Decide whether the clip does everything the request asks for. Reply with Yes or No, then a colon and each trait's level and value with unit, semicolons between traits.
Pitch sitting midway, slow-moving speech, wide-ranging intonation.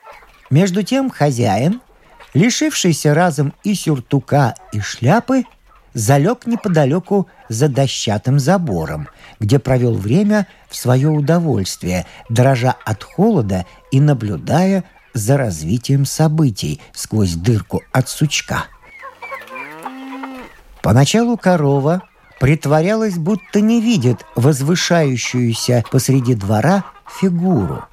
Yes: medium, 145 Hz; slow, 90 wpm; wide, 7.1 semitones